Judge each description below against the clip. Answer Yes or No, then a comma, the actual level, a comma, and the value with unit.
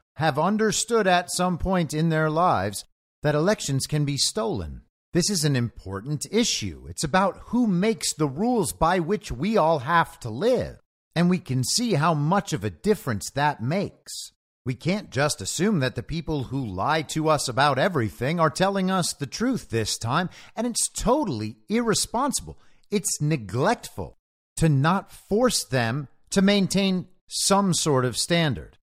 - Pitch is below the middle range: No, medium, 160 Hz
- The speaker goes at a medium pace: Yes, average, 160 wpm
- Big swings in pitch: Yes, wide, 7.0 semitones